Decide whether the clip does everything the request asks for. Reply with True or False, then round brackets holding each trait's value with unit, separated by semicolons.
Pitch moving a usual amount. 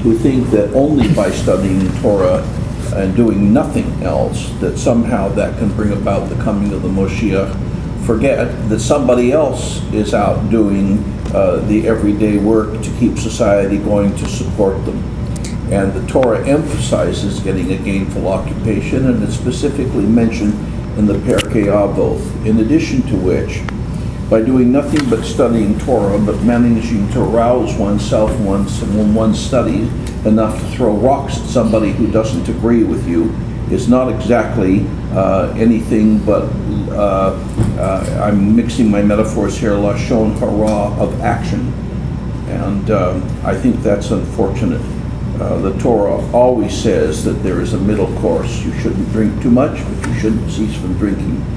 False (2.3 semitones)